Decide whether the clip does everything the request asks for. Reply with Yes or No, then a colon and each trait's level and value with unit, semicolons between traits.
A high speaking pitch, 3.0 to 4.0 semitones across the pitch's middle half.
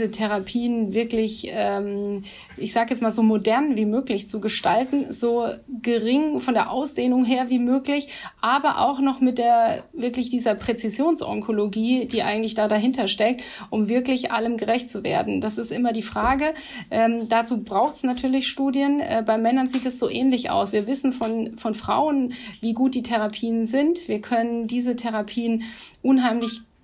No: high, 235 Hz; narrow, 2.6 semitones